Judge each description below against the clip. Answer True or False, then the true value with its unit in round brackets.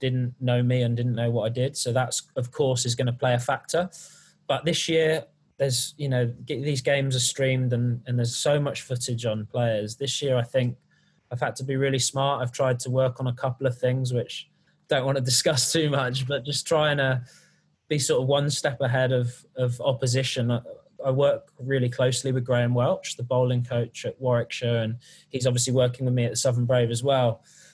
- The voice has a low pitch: True (130 Hz)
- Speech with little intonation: True (2.1 semitones)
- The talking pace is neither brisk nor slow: False (215 wpm)